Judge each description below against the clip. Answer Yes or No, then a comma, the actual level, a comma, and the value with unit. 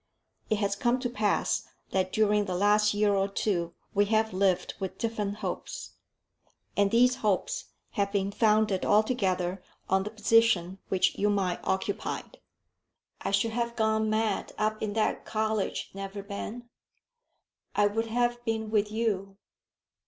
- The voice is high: Yes, high, 210 Hz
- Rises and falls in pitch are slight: Yes, narrow, 2.0 semitones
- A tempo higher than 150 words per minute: No, average, 145 wpm